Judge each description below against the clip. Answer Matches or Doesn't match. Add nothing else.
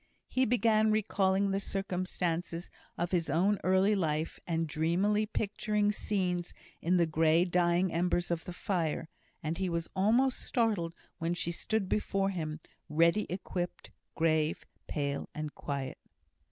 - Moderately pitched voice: Matches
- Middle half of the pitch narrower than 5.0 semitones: Matches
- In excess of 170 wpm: Doesn't match